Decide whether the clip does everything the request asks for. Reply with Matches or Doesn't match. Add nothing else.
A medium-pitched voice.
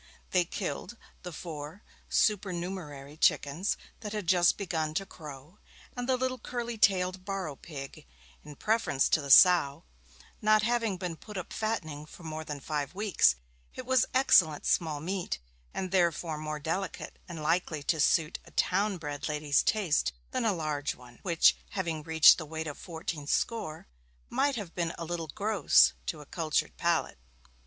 Matches